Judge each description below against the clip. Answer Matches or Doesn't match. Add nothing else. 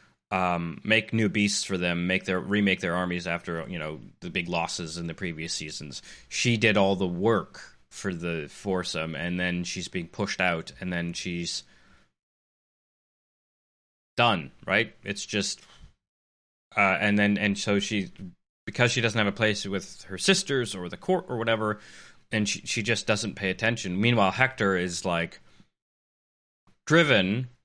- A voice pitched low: Matches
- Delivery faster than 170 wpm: Doesn't match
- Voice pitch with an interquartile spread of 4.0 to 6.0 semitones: Doesn't match